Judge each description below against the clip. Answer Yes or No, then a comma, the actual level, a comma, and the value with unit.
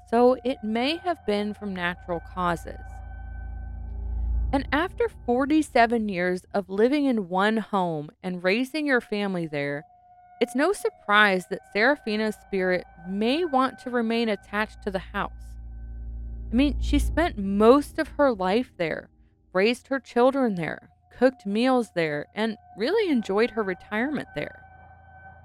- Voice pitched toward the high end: Yes, high, 215 Hz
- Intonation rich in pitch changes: Yes, wide, 6.5 semitones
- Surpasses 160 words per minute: No, slow, 135 wpm